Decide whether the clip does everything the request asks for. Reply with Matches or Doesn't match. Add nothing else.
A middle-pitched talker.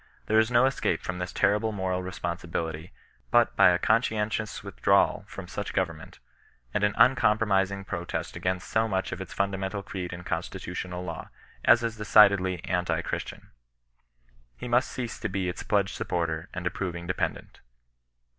Doesn't match